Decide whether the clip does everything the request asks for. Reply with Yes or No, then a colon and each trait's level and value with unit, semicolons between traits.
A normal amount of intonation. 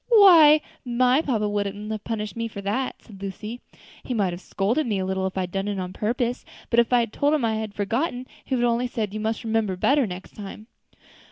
Yes: average, 3.6 semitones